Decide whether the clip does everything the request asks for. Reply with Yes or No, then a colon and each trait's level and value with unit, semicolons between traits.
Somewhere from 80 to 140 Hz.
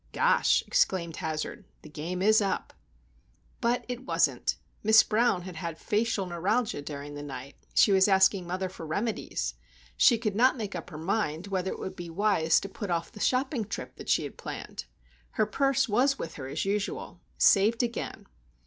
No: high, 195 Hz